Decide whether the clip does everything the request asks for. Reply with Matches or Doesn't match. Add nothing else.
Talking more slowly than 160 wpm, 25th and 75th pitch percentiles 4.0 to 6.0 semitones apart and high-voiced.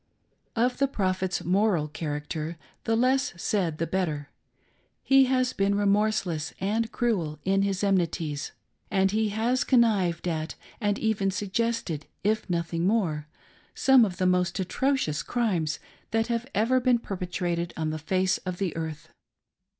Matches